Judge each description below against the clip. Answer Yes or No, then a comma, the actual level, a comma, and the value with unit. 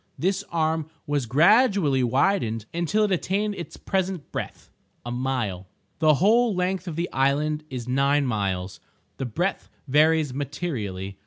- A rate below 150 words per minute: Yes, slow, 135 wpm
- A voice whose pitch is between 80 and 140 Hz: No, medium, 150 Hz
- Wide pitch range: Yes, wide, 6.2 semitones